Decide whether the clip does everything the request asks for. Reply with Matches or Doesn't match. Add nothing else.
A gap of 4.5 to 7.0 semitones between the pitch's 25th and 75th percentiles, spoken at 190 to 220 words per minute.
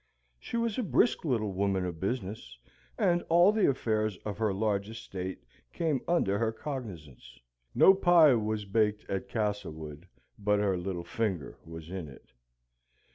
Doesn't match